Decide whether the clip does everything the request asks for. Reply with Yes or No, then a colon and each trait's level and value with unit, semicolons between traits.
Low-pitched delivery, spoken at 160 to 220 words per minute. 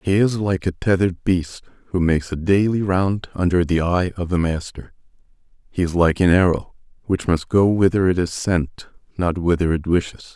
Yes: very low, 90 Hz; average, 190 wpm